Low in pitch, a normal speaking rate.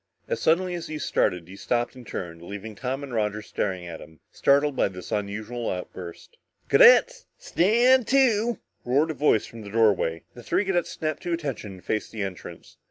Yes: low, 120 Hz; average, 190 wpm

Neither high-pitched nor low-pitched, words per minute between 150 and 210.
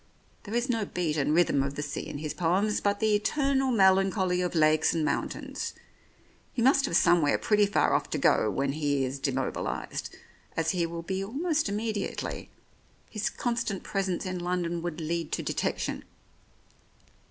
Yes: medium, 180 Hz; average, 170 wpm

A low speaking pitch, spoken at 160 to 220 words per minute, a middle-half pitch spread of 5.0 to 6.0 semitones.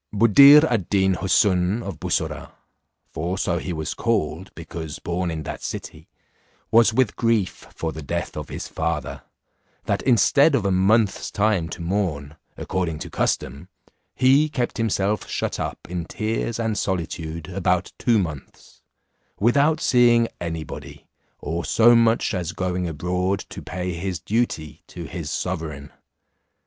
No: very low, 95 Hz; average, 145 wpm; average, 5.3 semitones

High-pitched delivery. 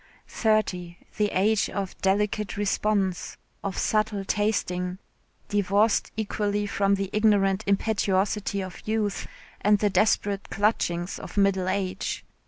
Yes: high, 200 Hz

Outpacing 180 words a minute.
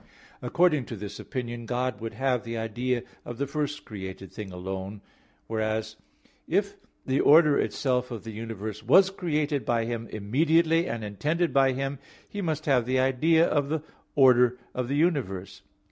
No: average, 160 wpm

